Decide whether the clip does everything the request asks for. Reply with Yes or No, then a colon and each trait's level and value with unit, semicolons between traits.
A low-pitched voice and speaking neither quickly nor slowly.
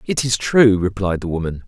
No: low, 100 Hz; fast, 215 wpm